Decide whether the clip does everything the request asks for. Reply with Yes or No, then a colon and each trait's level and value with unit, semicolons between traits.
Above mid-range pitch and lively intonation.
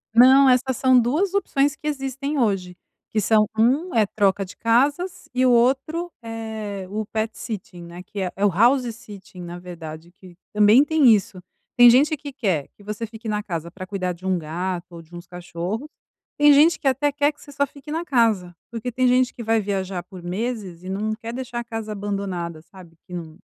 Yes: high, 220 Hz; wide, 5.9 semitones